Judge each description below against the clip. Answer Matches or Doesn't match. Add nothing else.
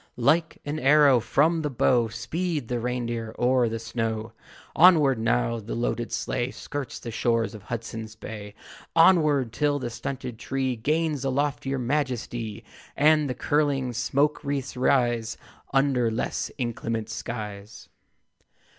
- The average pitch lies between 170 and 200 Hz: Doesn't match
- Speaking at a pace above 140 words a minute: Doesn't match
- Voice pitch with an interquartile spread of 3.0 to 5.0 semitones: Matches